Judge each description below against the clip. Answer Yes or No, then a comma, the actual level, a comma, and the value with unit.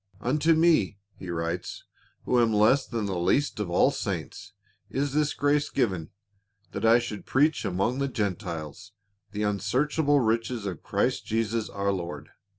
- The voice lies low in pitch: Yes, low, 110 Hz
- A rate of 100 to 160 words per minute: Yes, average, 155 wpm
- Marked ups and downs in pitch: Yes, wide, 6.0 semitones